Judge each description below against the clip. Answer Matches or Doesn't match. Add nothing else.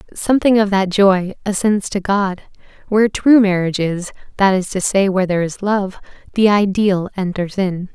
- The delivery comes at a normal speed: Matches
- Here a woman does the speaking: Matches